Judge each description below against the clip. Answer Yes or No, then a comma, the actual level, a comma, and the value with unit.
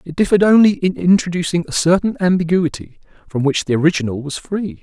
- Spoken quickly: No, average, 175 wpm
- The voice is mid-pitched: Yes, medium, 170 Hz